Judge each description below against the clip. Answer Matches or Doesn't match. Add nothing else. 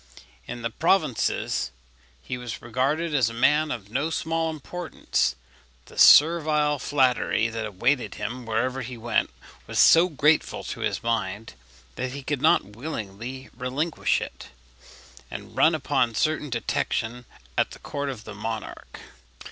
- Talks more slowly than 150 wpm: Matches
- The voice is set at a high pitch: Doesn't match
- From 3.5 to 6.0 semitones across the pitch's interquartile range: Matches